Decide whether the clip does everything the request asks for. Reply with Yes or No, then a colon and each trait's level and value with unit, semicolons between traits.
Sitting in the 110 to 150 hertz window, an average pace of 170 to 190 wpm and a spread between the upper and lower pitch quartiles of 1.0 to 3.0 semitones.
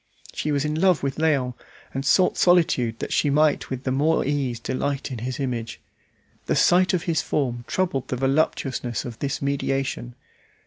No: medium, 140 Hz; average, 175 wpm; average, 3.4 semitones